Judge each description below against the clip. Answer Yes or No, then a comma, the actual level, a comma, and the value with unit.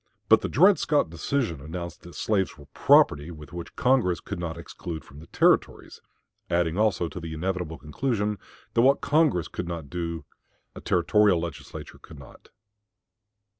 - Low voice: Yes, very low, 85 Hz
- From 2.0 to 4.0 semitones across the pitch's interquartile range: No, average, 4.4 semitones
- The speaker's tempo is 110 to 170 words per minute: Yes, average, 150 wpm